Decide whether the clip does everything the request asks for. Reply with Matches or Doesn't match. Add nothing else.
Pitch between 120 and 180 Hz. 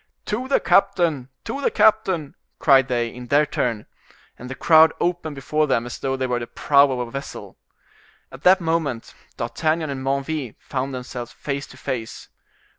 Matches